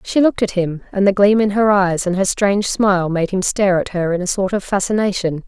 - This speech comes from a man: No, female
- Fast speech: Yes, fast, 265 wpm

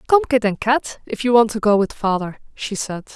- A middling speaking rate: No, fast, 245 wpm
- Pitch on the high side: Yes, high, 225 Hz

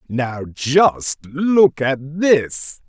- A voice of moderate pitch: Yes, medium, 145 Hz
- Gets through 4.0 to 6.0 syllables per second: No, 2.1 syllables/s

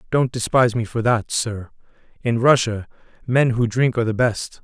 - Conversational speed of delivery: Yes, average, 180 wpm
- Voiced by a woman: No, male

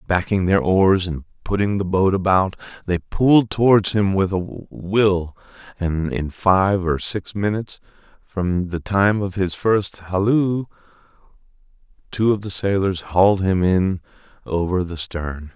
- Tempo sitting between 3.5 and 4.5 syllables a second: Yes, 4.0 syllables/s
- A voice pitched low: Yes, very low, 95 Hz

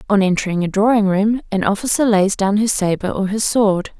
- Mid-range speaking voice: No, high, 205 Hz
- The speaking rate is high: Yes, fast, 210 wpm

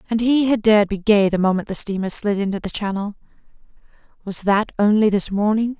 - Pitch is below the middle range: No, high, 205 Hz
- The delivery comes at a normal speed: Yes, average, 195 wpm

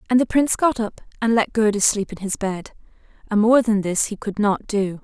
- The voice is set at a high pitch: Yes, high, 215 Hz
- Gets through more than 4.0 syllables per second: Yes, 5.3 syllables/s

